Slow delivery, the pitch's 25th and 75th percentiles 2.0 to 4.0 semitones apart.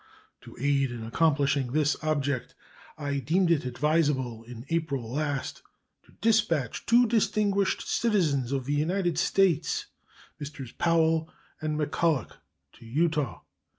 Yes: slow, 120 wpm; average, 3.6 semitones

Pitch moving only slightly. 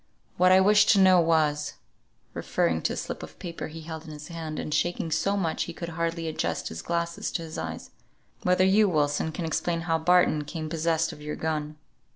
Yes: narrow, 2.1 semitones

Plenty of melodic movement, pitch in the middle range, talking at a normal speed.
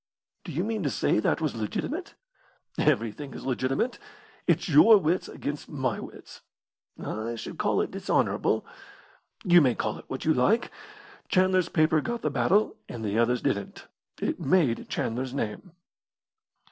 Yes: wide, 7.4 semitones; medium, 145 Hz; average, 150 wpm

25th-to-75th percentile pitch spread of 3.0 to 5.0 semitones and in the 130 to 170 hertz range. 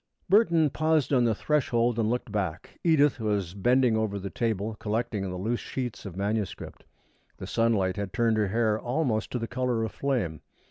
No: average, 3.6 semitones; low, 115 Hz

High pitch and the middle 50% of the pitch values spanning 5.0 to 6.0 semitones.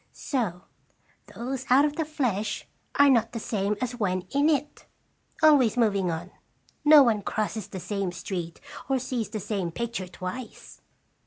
Yes: high, 225 Hz; wide, 5.4 semitones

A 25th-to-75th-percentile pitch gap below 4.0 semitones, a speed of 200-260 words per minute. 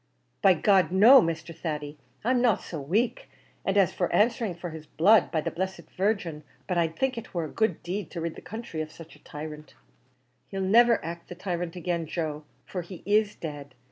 No: average, 4.3 semitones; fast, 205 wpm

